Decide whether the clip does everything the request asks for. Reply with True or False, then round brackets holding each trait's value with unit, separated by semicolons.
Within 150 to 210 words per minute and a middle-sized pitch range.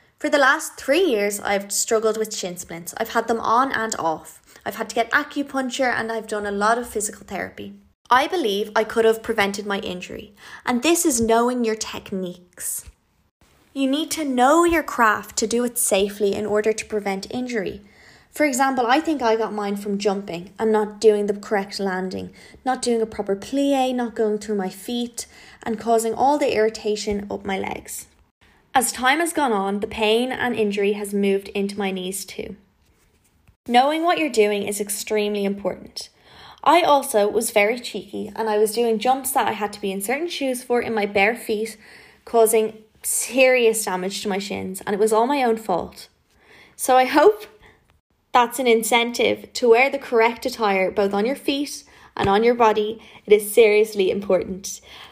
True (185 wpm; 3.3 semitones)